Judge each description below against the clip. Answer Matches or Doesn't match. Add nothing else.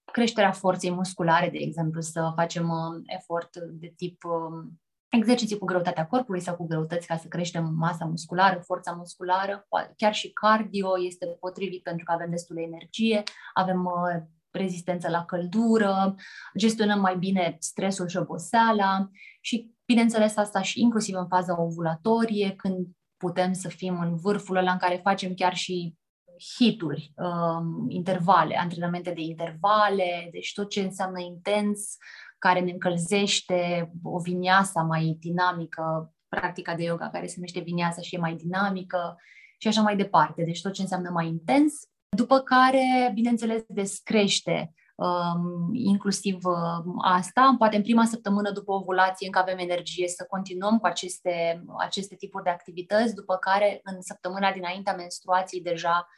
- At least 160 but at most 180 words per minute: Doesn't match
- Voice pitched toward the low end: Doesn't match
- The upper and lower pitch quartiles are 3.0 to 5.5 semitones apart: Doesn't match